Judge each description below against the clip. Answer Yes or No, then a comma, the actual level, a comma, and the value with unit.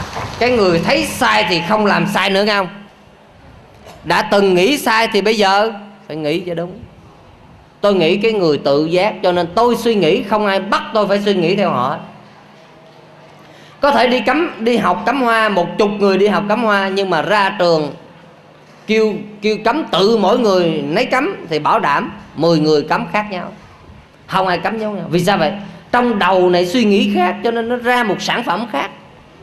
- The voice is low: No, high, 200 Hz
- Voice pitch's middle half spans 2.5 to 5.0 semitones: Yes, average, 3.8 semitones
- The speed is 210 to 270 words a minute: No, average, 200 wpm